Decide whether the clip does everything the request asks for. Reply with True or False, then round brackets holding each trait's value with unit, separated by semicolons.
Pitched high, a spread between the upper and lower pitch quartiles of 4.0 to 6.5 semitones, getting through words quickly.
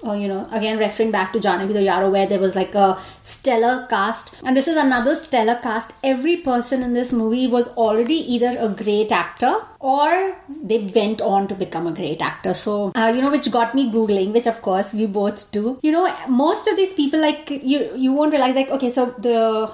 True (235 Hz; 4.3 semitones; 220 wpm)